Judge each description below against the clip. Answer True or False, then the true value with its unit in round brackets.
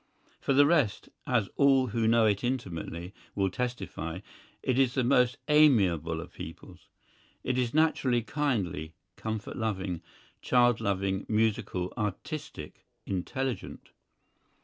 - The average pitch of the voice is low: True (115 Hz)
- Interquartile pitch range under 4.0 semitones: False (5.1 semitones)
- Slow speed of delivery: True (120 wpm)